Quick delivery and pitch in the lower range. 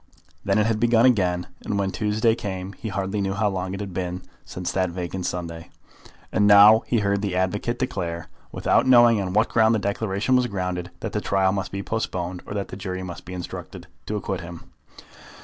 Yes: fast, 210 wpm; low, 100 Hz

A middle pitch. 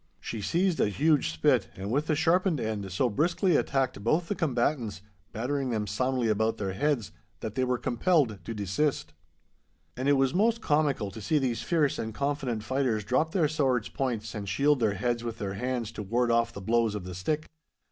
No: low, 125 Hz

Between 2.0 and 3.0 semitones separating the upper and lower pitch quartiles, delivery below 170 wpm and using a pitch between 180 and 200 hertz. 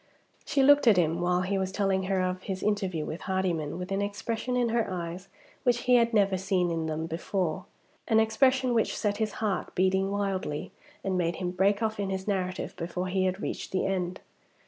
No: average, 2.7 semitones; fast, 205 wpm; high, 190 Hz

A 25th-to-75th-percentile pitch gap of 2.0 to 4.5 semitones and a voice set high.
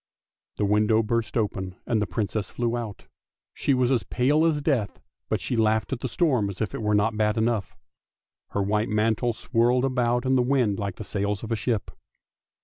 No: average, 2.8 semitones; low, 110 Hz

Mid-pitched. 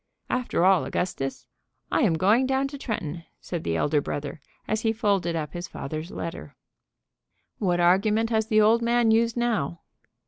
No: high, 195 Hz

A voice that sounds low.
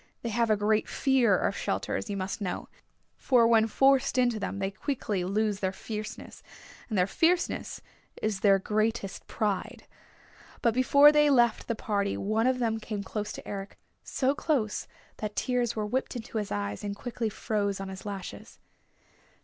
No: high, 215 Hz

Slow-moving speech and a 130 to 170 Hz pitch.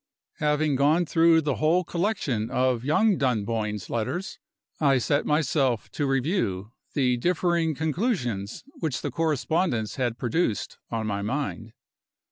Yes: slow, 125 wpm; medium, 140 Hz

